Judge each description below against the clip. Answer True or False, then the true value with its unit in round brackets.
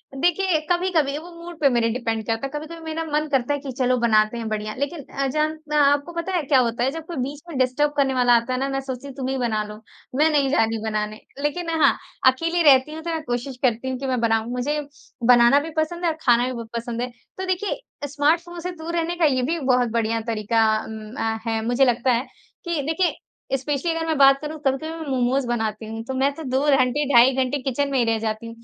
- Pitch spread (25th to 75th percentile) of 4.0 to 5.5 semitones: True (4.7 semitones)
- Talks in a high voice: True (270 Hz)